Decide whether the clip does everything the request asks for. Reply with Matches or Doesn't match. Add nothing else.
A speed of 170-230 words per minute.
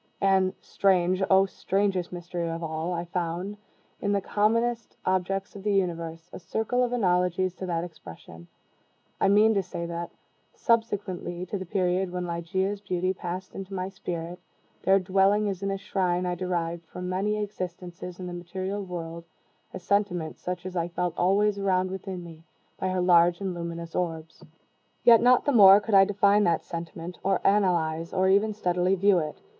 Matches